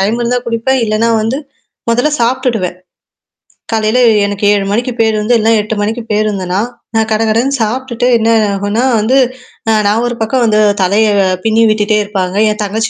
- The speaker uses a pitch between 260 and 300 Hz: No, high, 220 Hz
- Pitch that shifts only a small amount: Yes, narrow, 2.2 semitones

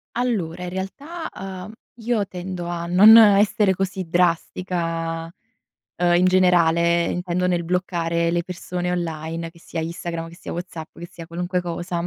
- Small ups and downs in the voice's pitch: Yes, narrow, 1.7 semitones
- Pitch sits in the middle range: Yes, medium, 175 Hz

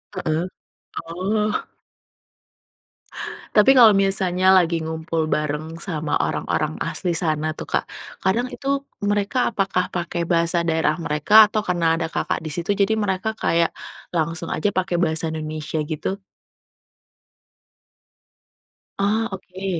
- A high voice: No, medium, 175 Hz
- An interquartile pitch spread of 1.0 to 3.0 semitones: No, average, 3.6 semitones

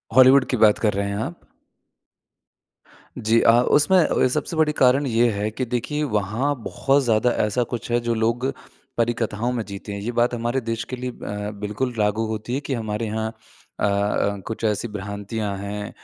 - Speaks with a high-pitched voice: No, low, 115 Hz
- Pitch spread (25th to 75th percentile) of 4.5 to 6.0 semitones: No, average, 3.1 semitones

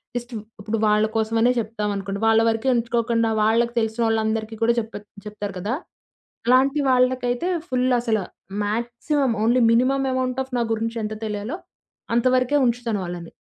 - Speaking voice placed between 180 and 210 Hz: No, high, 230 Hz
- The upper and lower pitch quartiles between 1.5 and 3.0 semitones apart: Yes, narrow, 2.4 semitones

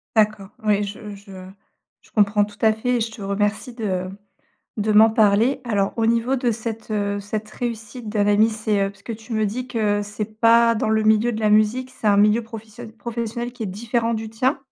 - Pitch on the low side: No, high, 220 Hz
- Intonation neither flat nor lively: No, narrow, 2.0 semitones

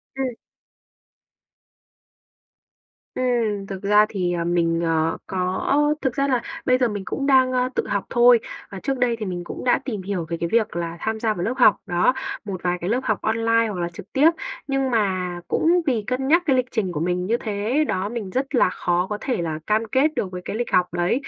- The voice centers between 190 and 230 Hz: Yes, high, 210 Hz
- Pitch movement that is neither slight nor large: No, wide, 5.7 semitones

